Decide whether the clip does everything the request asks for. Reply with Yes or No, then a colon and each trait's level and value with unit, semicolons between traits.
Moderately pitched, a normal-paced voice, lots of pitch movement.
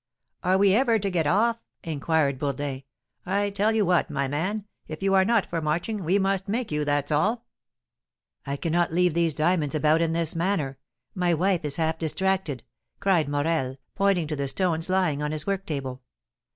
No: medium, 170 Hz; average, 185 wpm; average, 4.5 semitones